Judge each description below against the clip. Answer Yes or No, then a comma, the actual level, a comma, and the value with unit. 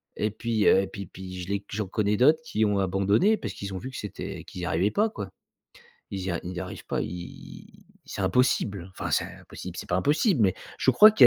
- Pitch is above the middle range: No, low, 100 Hz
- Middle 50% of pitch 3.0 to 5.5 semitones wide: Yes, average, 4.1 semitones